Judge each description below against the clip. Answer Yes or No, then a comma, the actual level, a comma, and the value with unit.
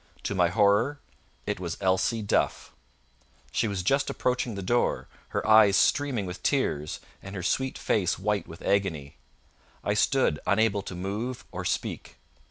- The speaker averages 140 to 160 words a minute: Yes, average, 155 wpm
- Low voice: Yes, low, 100 Hz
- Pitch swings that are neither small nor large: Yes, average, 3.8 semitones